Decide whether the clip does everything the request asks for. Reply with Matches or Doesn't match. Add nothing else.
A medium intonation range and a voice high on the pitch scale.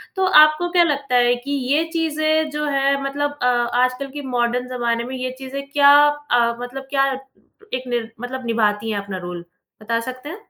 Matches